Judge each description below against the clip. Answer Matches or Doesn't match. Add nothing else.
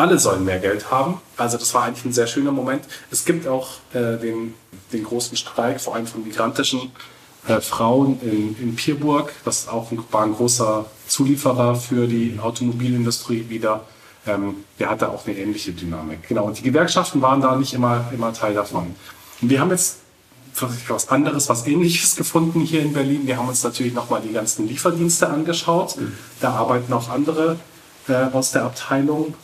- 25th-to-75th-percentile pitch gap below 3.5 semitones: Doesn't match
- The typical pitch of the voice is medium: Doesn't match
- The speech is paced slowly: Doesn't match